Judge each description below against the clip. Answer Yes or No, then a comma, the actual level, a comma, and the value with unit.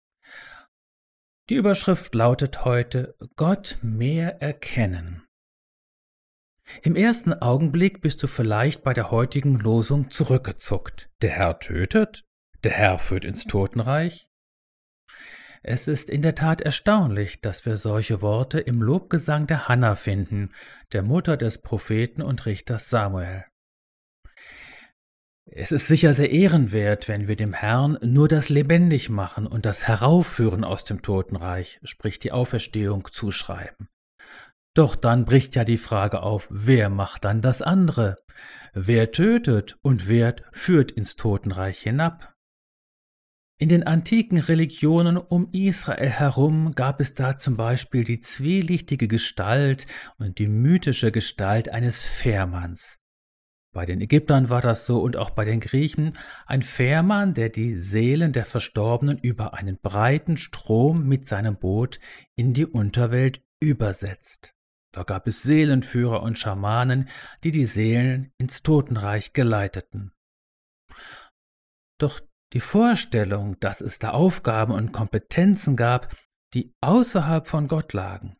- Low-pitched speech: Yes, low, 120 Hz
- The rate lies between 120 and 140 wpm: Yes, average, 130 wpm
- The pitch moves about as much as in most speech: No, wide, 6.0 semitones